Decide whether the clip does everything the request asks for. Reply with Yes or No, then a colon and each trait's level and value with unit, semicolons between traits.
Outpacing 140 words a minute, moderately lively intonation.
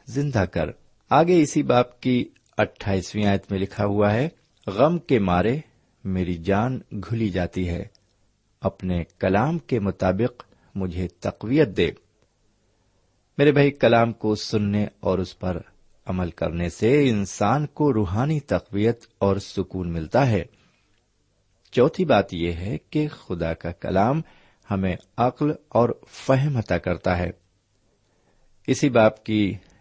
No: average, 130 wpm; average, 4.7 semitones